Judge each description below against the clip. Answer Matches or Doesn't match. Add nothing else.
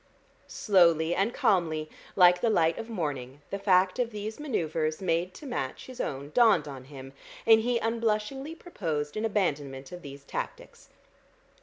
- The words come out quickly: Doesn't match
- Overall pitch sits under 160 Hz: Doesn't match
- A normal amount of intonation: Doesn't match